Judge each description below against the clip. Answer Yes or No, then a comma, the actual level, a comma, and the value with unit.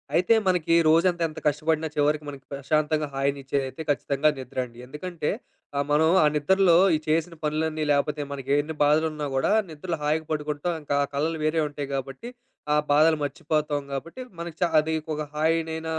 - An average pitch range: No, narrow, 2.0 semitones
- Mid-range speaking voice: Yes, medium, 150 Hz